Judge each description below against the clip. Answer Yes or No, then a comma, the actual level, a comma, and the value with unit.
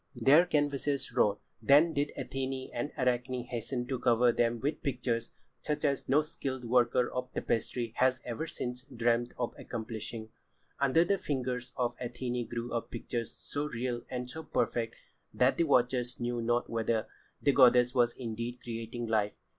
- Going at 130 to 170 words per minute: Yes, average, 160 wpm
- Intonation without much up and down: Yes, narrow, 2.1 semitones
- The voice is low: Yes, low, 125 Hz